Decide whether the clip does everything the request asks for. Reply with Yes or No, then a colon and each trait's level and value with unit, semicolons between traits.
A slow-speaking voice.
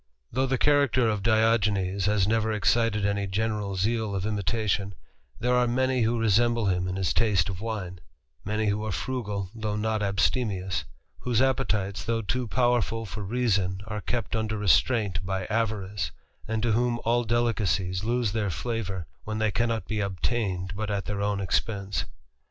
No: average, 165 wpm